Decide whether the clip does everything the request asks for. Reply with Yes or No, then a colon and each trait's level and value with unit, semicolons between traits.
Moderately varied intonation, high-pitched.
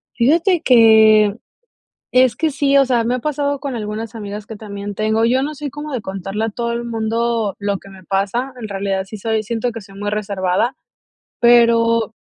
Yes: average, 3.2 semitones; high, 225 Hz